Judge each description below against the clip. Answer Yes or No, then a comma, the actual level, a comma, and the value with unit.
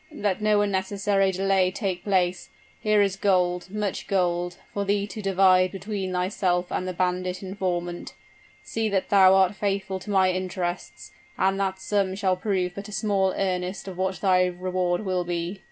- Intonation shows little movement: Yes, narrow, 1.5 semitones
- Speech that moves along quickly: No, average, 170 wpm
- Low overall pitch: No, high, 190 Hz